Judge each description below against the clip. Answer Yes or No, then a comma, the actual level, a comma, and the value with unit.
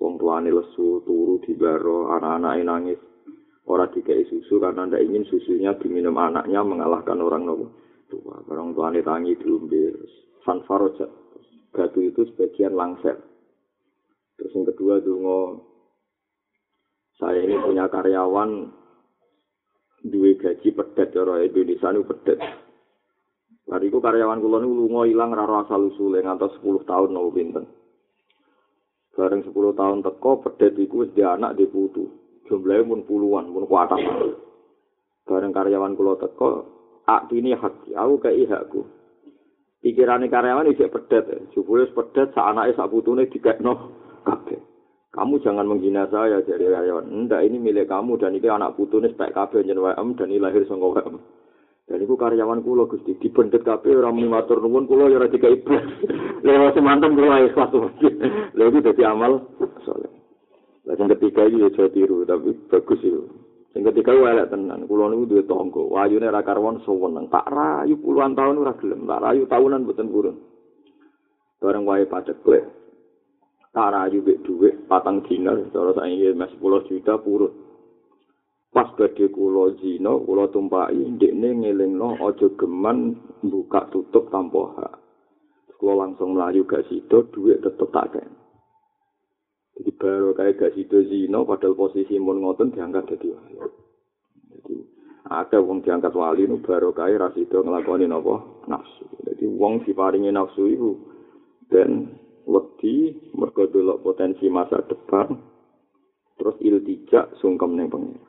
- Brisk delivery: Yes, fast, 145 wpm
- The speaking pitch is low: No, very high, 305 Hz